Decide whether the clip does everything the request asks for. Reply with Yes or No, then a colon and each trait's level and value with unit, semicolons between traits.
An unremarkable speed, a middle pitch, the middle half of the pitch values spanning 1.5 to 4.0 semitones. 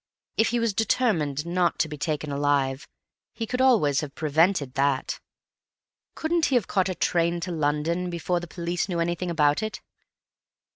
No: average, 165 wpm; medium, 170 Hz; average, 4.4 semitones